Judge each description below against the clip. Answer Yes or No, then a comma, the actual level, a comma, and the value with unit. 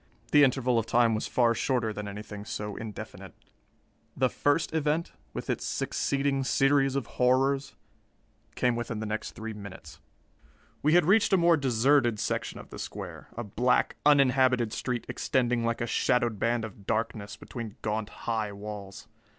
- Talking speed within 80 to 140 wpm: No, average, 160 wpm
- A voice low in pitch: Yes, low, 120 Hz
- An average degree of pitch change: Yes, average, 3.9 semitones